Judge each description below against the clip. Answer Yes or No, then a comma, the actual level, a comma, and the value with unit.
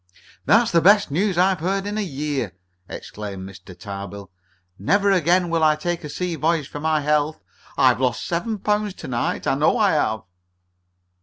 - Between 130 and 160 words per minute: No, average, 175 wpm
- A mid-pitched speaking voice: Yes, medium, 160 Hz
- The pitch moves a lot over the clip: Yes, wide, 6.7 semitones